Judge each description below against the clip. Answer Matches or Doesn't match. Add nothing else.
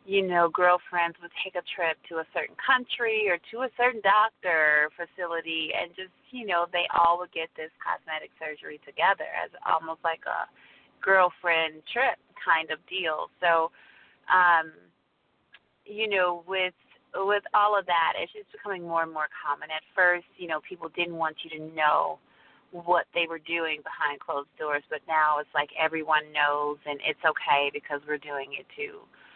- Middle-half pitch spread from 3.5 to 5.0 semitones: Doesn't match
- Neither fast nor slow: Matches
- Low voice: Doesn't match